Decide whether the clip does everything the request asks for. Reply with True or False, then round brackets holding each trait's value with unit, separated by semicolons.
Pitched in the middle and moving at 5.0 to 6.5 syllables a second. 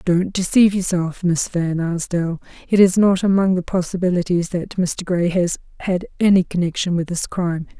True (180 Hz; 5.1 syllables/s)